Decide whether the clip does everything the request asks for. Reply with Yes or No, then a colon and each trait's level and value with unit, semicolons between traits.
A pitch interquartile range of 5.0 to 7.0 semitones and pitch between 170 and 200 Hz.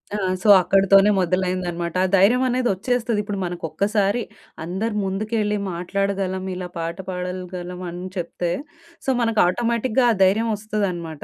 No: average, 3.1 semitones; high, 195 Hz